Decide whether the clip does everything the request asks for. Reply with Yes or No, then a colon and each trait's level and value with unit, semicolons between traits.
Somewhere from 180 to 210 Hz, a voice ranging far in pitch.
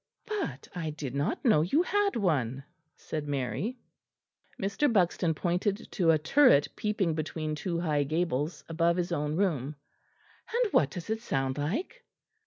No: medium, 170 Hz; wide, 5.9 semitones